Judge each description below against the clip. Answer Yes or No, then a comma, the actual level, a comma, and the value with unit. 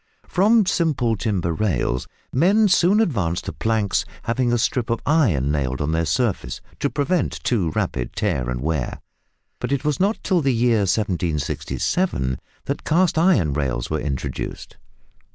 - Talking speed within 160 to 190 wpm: No, average, 150 wpm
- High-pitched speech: No, low, 110 Hz